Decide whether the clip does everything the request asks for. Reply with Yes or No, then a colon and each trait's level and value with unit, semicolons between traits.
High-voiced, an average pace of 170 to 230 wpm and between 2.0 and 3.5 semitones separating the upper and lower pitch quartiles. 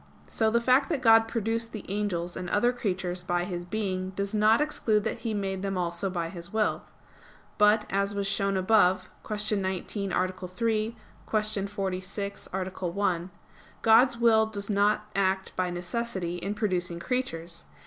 No: high, 200 Hz; average, 160 wpm; average, 3.0 semitones